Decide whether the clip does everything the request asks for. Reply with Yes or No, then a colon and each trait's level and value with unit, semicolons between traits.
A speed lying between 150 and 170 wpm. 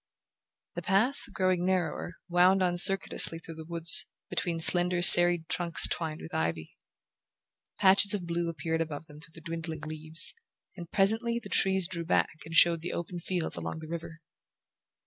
Yes: average, 165 wpm